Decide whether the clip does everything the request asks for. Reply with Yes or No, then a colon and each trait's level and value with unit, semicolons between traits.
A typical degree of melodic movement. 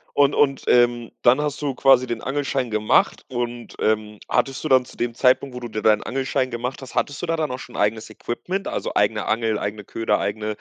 Yes: average, 3.6 semitones